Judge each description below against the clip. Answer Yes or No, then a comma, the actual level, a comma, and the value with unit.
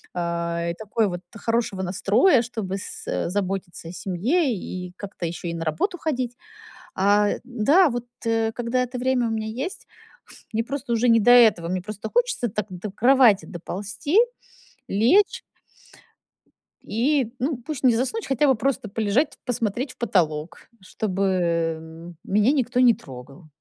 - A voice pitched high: Yes, high, 220 Hz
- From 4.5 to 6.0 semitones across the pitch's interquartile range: Yes, average, 5.2 semitones